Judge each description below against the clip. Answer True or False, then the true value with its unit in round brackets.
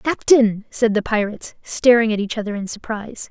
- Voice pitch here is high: True (220 Hz)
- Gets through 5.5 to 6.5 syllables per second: True (5.7 syllables/s)